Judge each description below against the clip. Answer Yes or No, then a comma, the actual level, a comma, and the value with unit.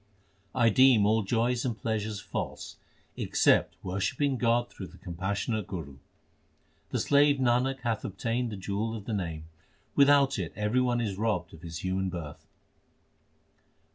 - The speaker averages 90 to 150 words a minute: Yes, average, 140 wpm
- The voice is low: Yes, low, 110 Hz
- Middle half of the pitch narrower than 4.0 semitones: No, average, 4.3 semitones